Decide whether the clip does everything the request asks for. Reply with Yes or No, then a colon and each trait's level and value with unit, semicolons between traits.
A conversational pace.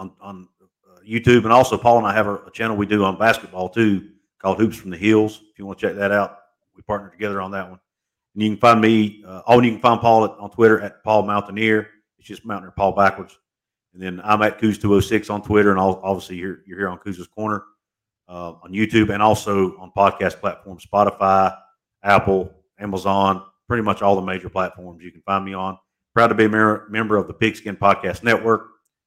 No: fast, 220 wpm